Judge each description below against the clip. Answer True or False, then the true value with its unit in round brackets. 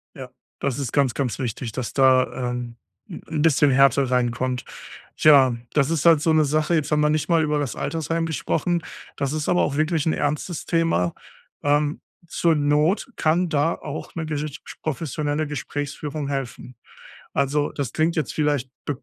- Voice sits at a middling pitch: True (150 Hz)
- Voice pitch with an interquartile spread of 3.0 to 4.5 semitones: False (2.6 semitones)